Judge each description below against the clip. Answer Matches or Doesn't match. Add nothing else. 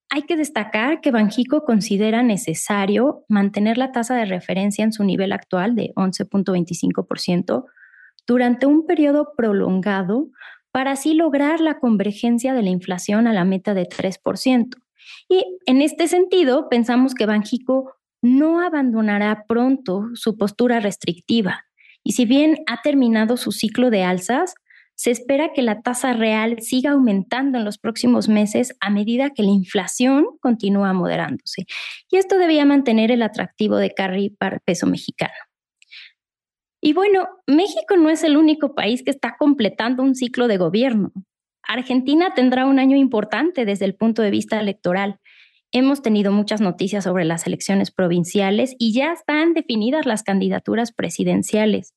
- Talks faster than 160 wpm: Doesn't match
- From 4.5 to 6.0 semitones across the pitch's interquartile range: Matches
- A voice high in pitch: Matches